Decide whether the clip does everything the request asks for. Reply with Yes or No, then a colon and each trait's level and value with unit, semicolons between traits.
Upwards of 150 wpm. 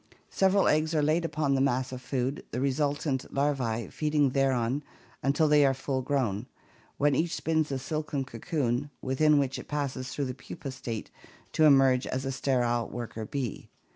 Yes: average, 175 wpm